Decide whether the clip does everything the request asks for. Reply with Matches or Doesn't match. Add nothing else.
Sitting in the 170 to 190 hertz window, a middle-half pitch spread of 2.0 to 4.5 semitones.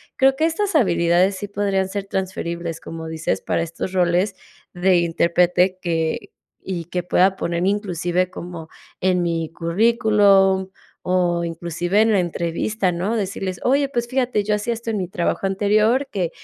Matches